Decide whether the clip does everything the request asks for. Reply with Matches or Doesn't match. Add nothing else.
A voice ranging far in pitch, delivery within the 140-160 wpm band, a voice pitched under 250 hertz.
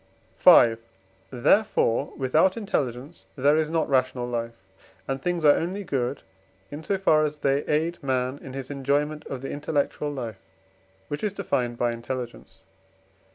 Doesn't match